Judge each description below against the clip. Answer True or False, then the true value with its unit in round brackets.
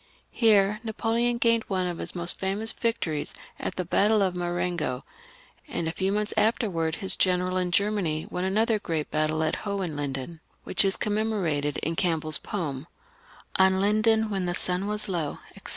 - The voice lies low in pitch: False (185 Hz)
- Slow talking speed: False (170 wpm)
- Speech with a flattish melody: False (4.2 semitones)